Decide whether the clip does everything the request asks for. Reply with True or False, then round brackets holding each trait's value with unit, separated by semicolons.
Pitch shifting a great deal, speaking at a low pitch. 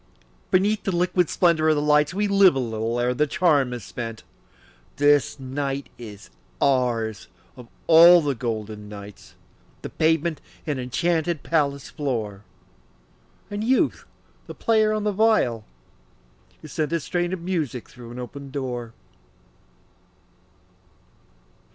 False (6.1 semitones; 145 Hz)